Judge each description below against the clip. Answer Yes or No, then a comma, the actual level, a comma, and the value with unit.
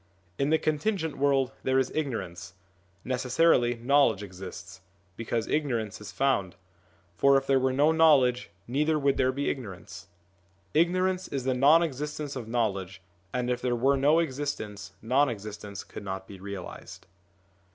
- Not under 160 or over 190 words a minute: No, average, 150 wpm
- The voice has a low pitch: Yes, low, 130 Hz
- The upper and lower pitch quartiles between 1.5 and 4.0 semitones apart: No, wide, 5.5 semitones